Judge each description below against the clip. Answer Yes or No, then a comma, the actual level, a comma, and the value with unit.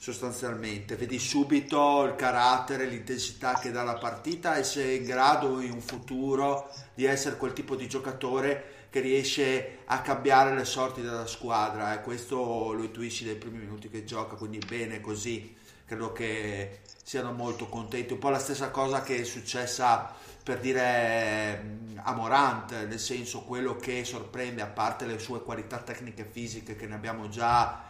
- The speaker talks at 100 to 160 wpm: No, fast, 170 wpm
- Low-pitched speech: Yes, low, 120 Hz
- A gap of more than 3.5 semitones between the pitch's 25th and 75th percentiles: No, average, 2.7 semitones